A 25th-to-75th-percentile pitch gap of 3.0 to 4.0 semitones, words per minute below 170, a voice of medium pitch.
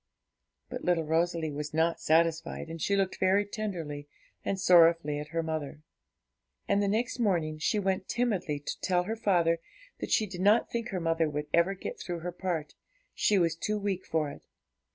No: average, 3.6 semitones; average, 180 wpm; medium, 175 Hz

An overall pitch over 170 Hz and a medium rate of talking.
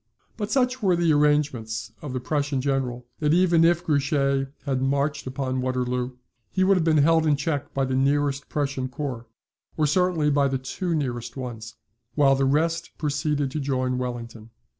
No: medium, 140 Hz; average, 175 wpm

